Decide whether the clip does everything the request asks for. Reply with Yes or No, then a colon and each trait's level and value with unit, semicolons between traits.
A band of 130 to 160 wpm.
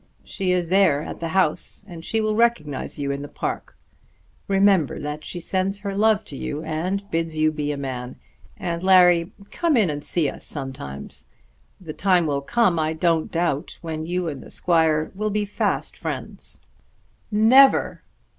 No: average, 175 wpm